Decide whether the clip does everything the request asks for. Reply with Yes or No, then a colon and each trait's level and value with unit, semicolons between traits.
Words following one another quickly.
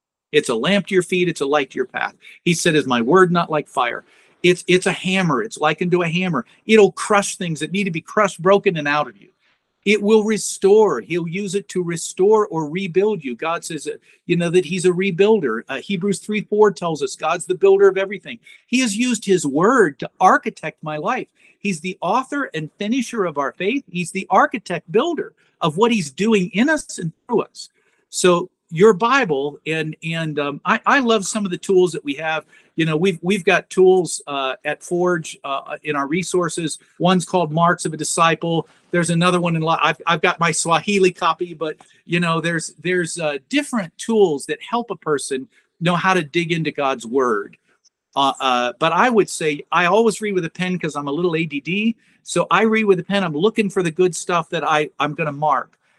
Yes: fast, 215 wpm